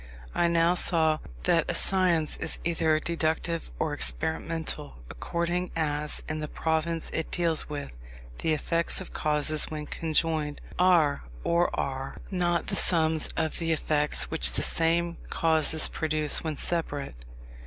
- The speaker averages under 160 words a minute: Yes, average, 140 wpm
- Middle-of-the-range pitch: Yes, medium, 160 Hz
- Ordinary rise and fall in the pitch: No, narrow, 1.8 semitones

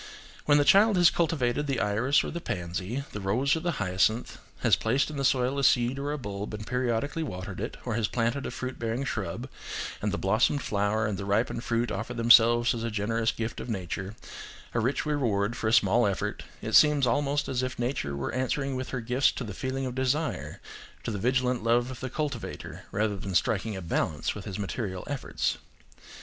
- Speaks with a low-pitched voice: Yes, low, 120 Hz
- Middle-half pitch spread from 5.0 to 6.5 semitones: No, average, 4.3 semitones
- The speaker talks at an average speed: No, fast, 210 wpm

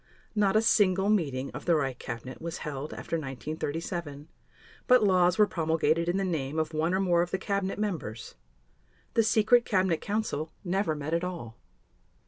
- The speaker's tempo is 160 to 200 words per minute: Yes, average, 170 wpm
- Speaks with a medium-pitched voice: Yes, medium, 170 Hz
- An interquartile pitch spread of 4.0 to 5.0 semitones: Yes, average, 4.4 semitones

